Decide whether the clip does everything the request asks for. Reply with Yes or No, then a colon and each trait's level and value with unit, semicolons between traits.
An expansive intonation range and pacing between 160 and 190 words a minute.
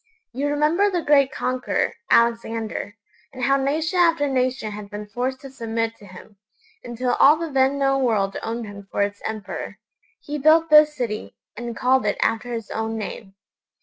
No: average, 4.2 semitones; average, 175 wpm